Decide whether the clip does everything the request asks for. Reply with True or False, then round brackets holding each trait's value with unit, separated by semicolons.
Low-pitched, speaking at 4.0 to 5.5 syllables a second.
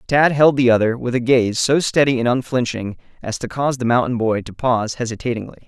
False (125 Hz; 6.0 syllables/s)